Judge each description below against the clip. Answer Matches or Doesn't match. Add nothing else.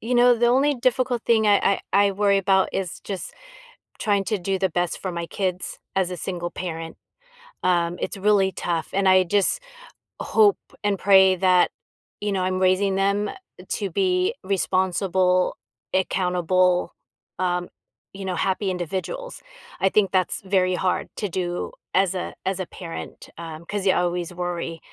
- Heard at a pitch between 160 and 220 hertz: Matches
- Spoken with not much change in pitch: Matches